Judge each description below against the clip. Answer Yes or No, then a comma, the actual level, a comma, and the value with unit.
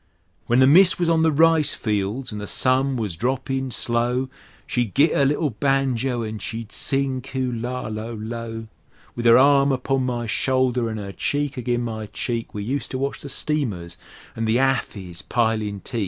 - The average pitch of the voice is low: Yes, low, 125 Hz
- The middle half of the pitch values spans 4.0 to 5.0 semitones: No, average, 3.2 semitones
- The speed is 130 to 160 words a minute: No, average, 175 wpm